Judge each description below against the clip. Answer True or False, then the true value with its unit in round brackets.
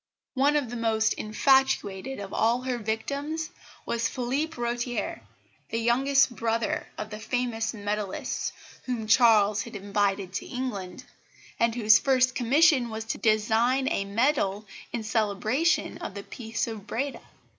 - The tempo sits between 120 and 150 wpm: True (140 wpm)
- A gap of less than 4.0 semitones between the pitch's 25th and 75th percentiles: True (3.3 semitones)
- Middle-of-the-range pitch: False (230 Hz)